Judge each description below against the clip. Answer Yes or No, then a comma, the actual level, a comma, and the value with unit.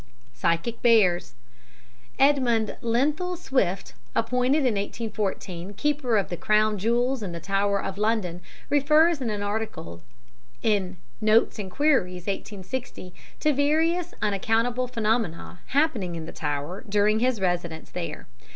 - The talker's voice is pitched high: Yes, high, 215 Hz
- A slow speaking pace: Yes, slow, 125 wpm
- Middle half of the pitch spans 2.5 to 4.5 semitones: No, average, 5.3 semitones